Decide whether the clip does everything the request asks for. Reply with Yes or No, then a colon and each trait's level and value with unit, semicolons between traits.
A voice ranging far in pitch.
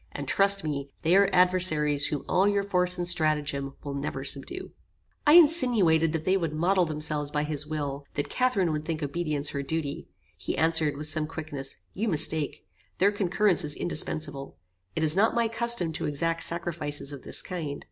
No: average, 3.8 semitones